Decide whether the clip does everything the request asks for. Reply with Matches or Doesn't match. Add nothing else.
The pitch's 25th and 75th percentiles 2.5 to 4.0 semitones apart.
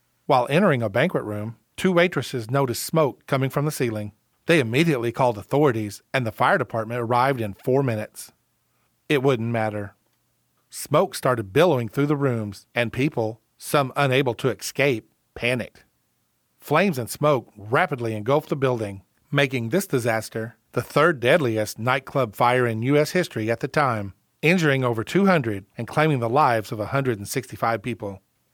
Doesn't match